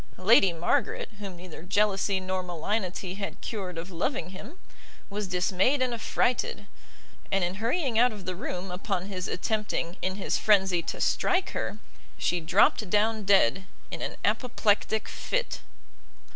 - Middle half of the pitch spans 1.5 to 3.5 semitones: Yes, average, 3.2 semitones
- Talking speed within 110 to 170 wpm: Yes, average, 145 wpm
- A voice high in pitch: Yes, high, 195 Hz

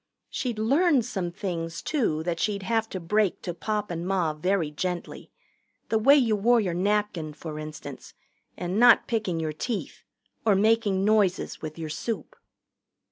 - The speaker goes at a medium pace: Yes, average, 160 wpm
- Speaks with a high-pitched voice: Yes, high, 195 Hz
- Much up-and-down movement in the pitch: No, average, 4.8 semitones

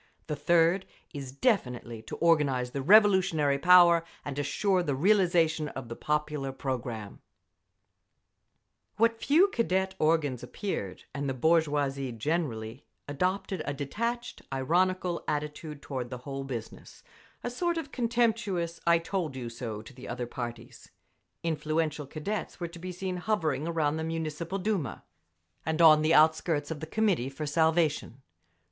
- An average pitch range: Yes, average, 4.9 semitones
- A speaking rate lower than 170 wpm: Yes, slow, 135 wpm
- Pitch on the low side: No, medium, 155 Hz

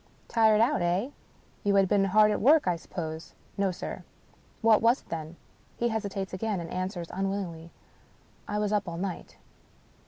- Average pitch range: Yes, average, 3.4 semitones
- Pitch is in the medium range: No, high, 195 Hz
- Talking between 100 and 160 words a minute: No, average, 190 wpm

